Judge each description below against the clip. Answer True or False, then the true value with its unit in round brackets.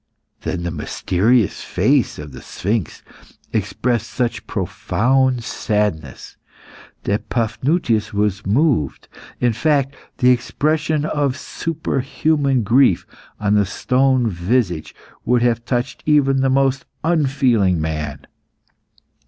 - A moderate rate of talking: False (105 wpm)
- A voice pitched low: True (120 Hz)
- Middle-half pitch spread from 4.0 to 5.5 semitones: True (5.1 semitones)